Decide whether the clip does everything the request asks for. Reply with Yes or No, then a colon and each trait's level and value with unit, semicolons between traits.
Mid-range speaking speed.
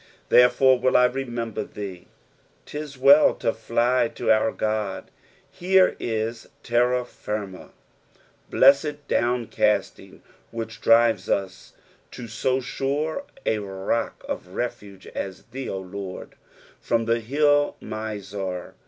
No: slow, 115 wpm